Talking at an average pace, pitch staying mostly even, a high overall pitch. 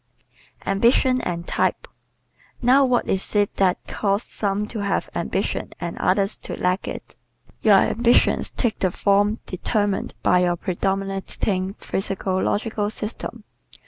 No: slow, 130 wpm; narrow, 2.3 semitones; high, 200 Hz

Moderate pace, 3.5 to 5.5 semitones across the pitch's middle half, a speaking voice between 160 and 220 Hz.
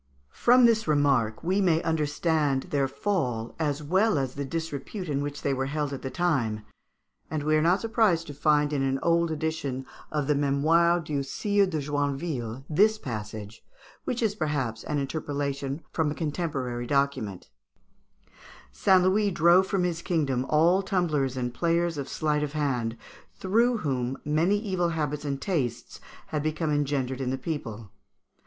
No: average, 165 wpm; average, 4.0 semitones; medium, 150 Hz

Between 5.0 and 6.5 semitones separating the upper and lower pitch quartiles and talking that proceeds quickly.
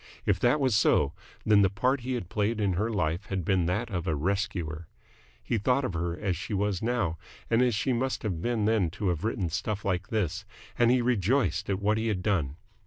No: average, 4.4 semitones; fast, 225 wpm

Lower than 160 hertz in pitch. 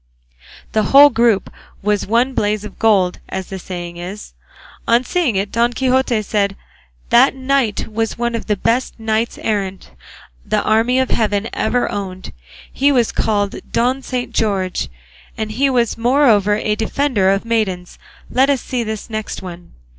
No: high, 220 Hz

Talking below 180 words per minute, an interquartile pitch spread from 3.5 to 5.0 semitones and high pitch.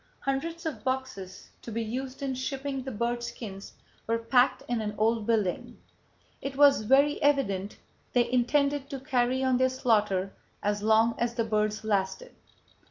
Yes: average, 160 wpm; average, 3.8 semitones; high, 240 Hz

